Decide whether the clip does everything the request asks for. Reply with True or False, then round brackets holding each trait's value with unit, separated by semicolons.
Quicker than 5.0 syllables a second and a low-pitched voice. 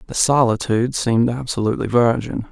True (6.0 syllables/s; 115 Hz)